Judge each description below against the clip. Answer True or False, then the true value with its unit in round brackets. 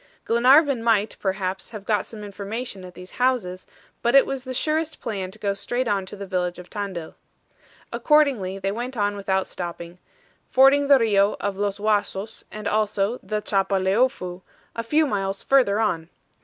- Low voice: False (205 Hz)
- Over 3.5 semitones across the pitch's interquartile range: True (4.0 semitones)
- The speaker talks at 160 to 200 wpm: True (170 wpm)